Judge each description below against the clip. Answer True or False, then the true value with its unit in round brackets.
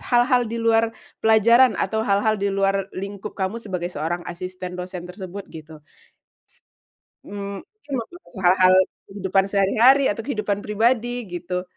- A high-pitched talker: True (200 Hz)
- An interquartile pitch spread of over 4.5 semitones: False (3.7 semitones)